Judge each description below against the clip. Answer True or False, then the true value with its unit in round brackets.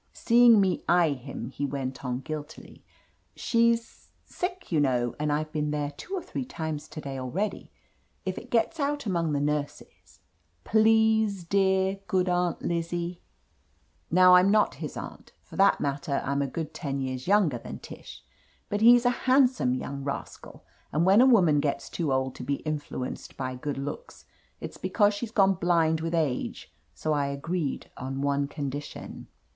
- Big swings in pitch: True (6.1 semitones)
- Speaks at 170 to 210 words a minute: True (175 wpm)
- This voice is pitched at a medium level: True (160 Hz)